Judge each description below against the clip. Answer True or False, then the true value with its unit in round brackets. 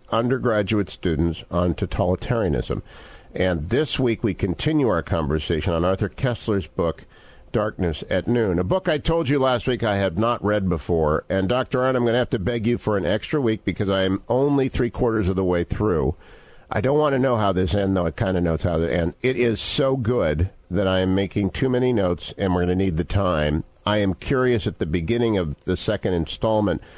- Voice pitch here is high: False (105 Hz)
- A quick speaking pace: True (220 wpm)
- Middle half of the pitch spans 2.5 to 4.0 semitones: False (5.2 semitones)